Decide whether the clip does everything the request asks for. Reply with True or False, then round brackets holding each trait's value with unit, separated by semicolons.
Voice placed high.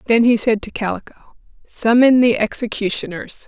True (225 Hz)